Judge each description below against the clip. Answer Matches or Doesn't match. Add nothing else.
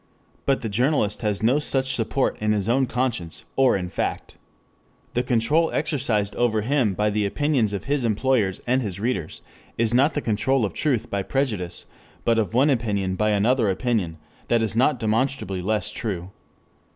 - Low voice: Matches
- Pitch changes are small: Doesn't match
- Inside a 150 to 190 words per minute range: Matches